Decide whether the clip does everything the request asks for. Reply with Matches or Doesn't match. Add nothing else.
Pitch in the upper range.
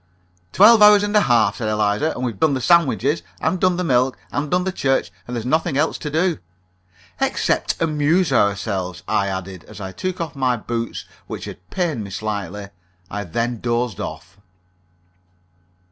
Doesn't match